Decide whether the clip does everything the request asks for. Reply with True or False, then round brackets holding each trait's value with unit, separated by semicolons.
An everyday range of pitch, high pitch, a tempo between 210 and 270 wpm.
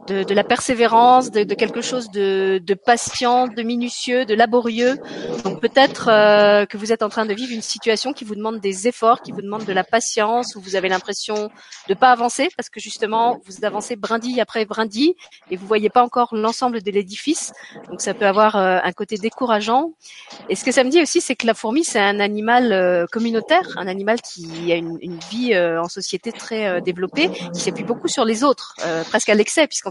True (3.2 semitones; 220 Hz; 220 wpm)